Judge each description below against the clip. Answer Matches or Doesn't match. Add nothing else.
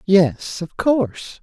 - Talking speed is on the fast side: Doesn't match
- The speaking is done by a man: Matches